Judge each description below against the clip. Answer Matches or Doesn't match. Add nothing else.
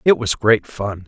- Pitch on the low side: Matches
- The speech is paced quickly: Matches